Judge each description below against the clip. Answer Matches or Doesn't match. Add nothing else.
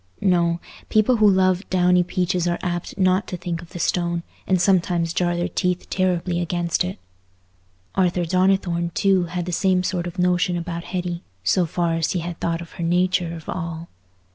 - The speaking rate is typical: Matches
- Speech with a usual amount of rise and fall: Doesn't match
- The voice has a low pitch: Doesn't match